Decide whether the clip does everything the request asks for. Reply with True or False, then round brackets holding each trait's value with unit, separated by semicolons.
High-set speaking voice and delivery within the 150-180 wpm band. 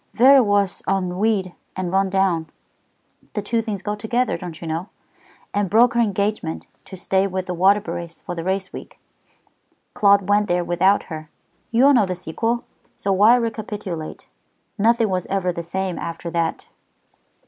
True (195 Hz; 160 wpm)